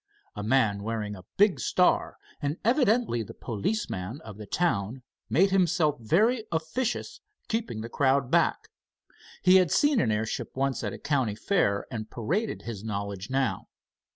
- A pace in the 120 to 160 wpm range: Yes, average, 155 wpm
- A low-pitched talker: Yes, low, 130 Hz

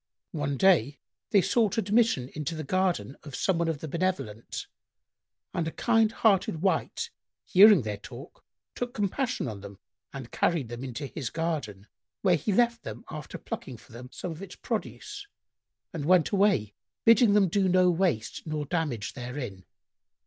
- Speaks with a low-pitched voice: No, medium, 165 Hz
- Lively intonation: Yes, wide, 6.7 semitones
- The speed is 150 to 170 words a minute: Yes, average, 165 wpm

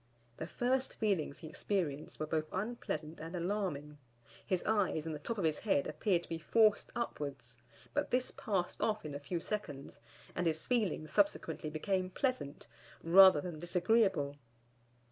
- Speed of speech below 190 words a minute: Yes, average, 160 wpm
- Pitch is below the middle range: No, medium, 175 Hz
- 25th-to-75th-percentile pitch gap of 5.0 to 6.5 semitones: Yes, wide, 5.4 semitones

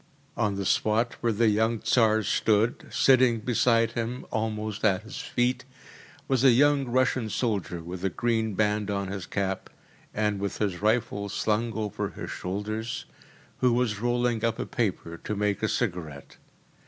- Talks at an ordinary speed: Yes, average, 160 wpm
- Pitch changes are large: No, average, 2.7 semitones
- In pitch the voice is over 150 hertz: No, low, 110 Hz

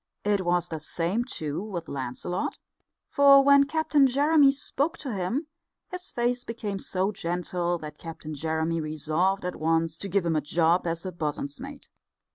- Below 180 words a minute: Yes, average, 160 wpm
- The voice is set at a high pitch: No, medium, 180 Hz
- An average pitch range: No, wide, 7.3 semitones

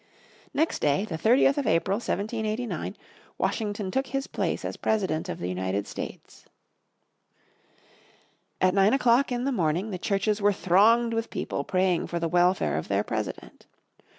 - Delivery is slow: No, average, 150 wpm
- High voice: Yes, high, 200 Hz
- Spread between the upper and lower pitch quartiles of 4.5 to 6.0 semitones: Yes, wide, 5.4 semitones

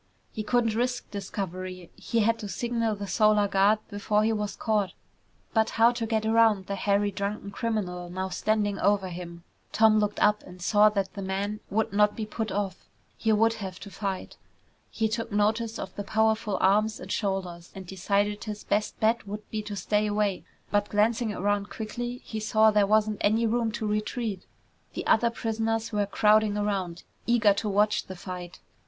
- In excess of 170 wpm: Yes, average, 185 wpm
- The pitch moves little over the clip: Yes, narrow, 1.8 semitones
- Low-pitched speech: No, high, 210 Hz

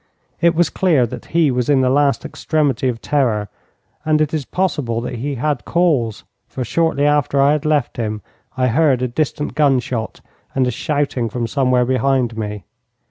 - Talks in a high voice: No, low, 135 Hz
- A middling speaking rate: Yes, average, 180 wpm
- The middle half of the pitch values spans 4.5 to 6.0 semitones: No, average, 3.6 semitones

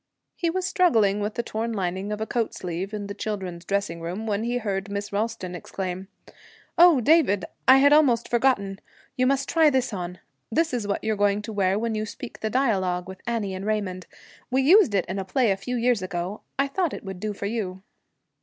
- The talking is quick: Yes, fast, 215 wpm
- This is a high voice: Yes, high, 210 Hz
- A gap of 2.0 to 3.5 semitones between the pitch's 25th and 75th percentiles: No, average, 4.3 semitones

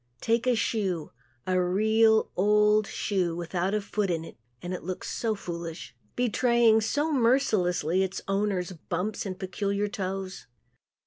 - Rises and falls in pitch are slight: No, average, 3.2 semitones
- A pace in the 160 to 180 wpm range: No, average, 140 wpm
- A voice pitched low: No, high, 195 Hz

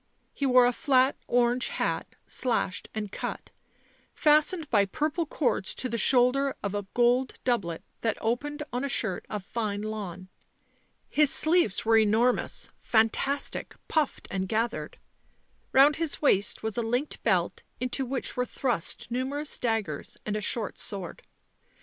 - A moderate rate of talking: Yes, average, 150 wpm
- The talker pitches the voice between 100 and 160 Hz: No, high, 245 Hz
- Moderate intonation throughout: Yes, average, 4.5 semitones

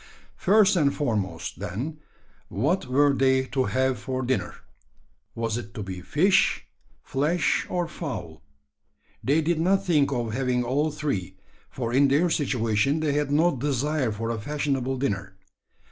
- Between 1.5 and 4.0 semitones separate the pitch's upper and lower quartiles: No, average, 4.5 semitones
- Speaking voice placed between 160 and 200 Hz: No, low, 135 Hz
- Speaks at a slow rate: No, average, 145 wpm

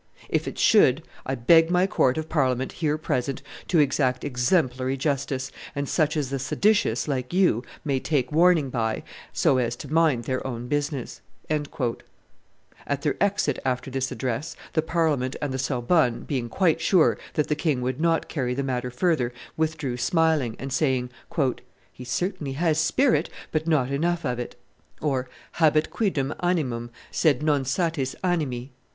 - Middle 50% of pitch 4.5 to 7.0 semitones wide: No, average, 3.9 semitones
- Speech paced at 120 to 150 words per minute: No, average, 160 wpm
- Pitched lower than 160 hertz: Yes, medium, 140 Hz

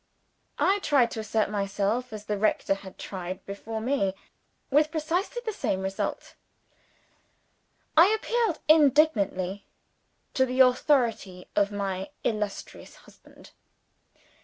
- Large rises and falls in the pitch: Yes, wide, 7.3 semitones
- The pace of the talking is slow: Yes, slow, 110 wpm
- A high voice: Yes, high, 220 Hz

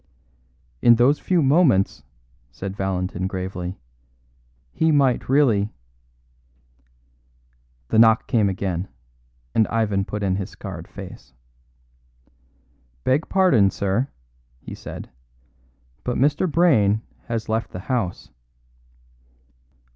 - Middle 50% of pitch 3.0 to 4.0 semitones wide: No, average, 5.3 semitones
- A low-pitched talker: Yes, low, 100 Hz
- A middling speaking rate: No, slow, 100 wpm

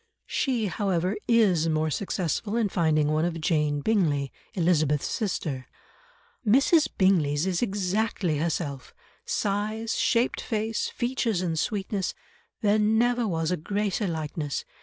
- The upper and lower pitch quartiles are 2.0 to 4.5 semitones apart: No, wide, 5.5 semitones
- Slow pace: Yes, slow, 115 wpm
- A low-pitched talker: No, medium, 185 Hz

